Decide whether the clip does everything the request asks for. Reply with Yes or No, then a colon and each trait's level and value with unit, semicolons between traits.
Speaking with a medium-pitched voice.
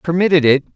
Yes: medium, 160 Hz